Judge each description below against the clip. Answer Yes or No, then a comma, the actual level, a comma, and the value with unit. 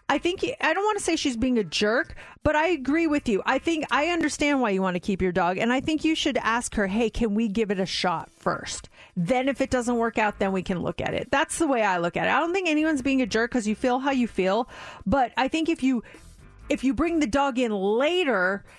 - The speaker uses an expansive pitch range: Yes, wide, 5.8 semitones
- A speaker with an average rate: No, fast, 275 wpm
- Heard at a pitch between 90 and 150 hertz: No, very high, 255 Hz